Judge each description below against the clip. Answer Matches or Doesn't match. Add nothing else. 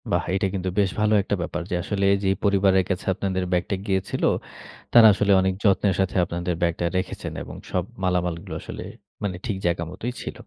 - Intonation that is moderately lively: Doesn't match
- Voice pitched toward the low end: Matches